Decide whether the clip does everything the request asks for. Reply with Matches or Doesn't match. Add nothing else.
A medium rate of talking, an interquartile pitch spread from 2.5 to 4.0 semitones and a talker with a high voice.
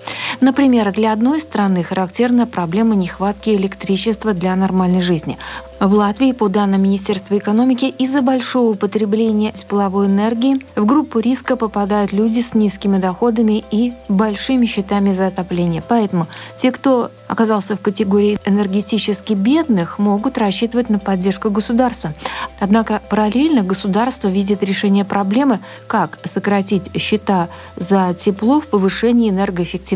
Matches